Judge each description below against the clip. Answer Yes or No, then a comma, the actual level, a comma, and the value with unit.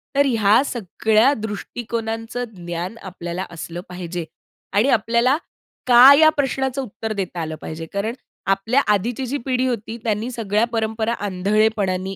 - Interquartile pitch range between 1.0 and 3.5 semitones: No, average, 4.0 semitones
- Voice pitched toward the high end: Yes, high, 220 Hz